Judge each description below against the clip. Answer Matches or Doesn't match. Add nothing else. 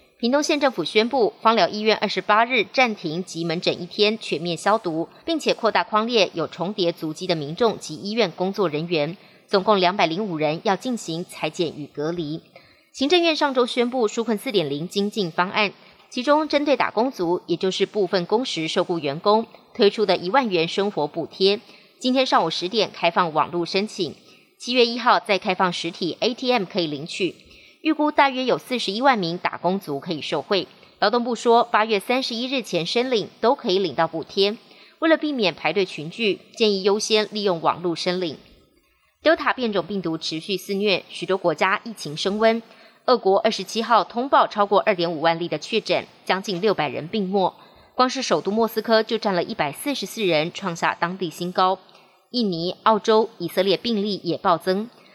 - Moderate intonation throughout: Matches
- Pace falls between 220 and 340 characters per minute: Matches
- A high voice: Matches